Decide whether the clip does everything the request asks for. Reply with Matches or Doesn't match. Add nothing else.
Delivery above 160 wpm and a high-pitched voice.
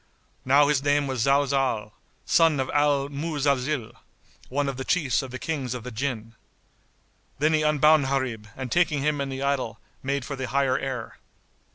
Doesn't match